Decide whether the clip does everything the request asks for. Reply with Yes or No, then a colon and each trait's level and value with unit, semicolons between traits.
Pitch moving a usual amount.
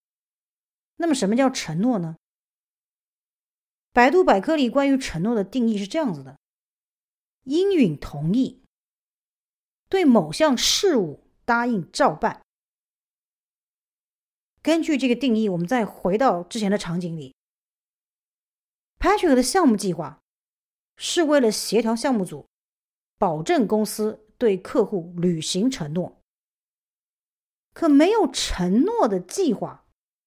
No: wide, 7.4 semitones